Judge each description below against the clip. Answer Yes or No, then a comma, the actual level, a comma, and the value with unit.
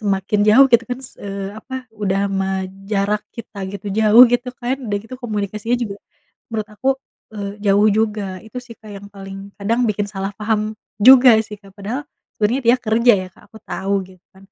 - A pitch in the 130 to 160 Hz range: No, high, 210 Hz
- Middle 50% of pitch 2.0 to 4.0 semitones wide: Yes, narrow, 2.6 semitones